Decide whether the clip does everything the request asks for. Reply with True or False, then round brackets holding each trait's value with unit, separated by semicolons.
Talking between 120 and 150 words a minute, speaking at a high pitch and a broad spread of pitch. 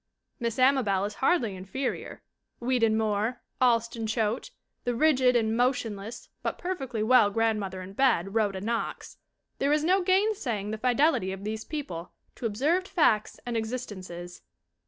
False (140 wpm; 230 Hz; 4.0 semitones)